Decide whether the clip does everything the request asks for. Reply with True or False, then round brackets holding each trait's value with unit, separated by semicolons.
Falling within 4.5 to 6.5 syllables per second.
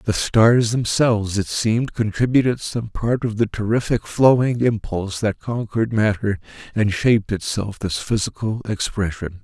True (4.7 syllables/s)